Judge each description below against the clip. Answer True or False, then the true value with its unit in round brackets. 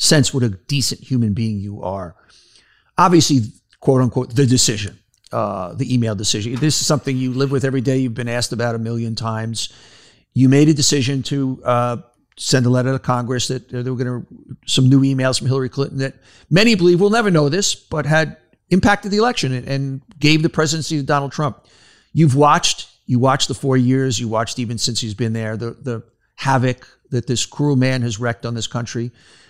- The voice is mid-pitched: False (130 Hz)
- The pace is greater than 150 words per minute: True (200 wpm)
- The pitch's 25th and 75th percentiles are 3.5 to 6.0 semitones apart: False (3.0 semitones)